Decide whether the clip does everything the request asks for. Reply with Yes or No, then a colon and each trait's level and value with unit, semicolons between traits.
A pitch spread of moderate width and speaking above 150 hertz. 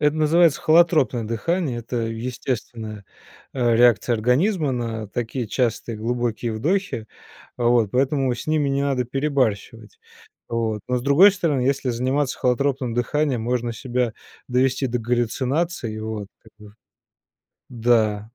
No: average, 3.4 semitones; low, 125 Hz